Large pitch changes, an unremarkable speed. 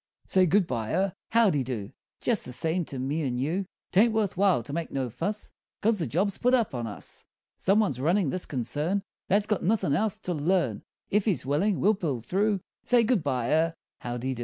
No: wide, 7.3 semitones; fast, 210 wpm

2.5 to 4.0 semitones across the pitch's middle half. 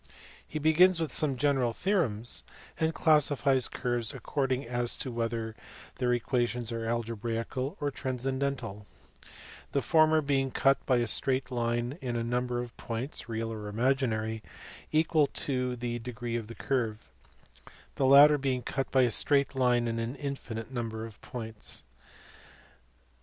Yes: average, 3.0 semitones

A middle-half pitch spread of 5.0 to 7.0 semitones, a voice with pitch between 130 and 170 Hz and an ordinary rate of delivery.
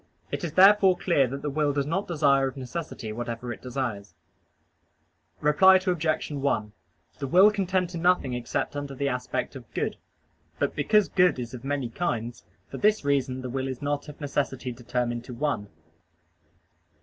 Yes: wide, 5.4 semitones; medium, 140 Hz; average, 175 wpm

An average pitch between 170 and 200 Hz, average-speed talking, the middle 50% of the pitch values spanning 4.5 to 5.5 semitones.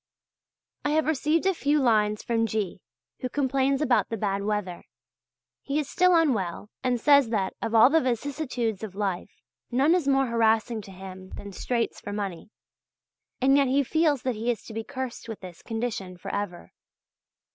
No: high, 235 Hz; average, 180 wpm; average, 5.0 semitones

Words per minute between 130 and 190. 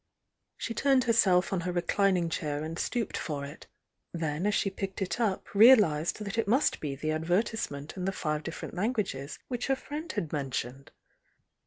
Yes: average, 180 wpm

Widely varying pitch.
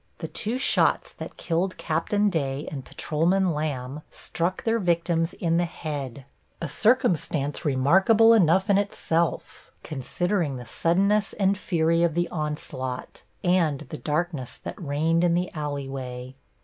No: average, 4.2 semitones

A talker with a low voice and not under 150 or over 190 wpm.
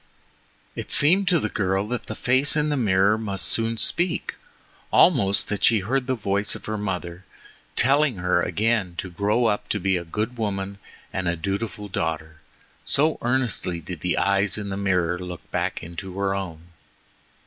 Yes: low, 100 Hz; average, 170 wpm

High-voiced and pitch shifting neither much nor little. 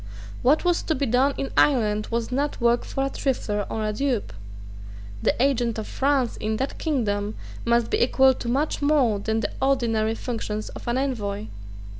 Yes: high, 240 Hz; average, 3.8 semitones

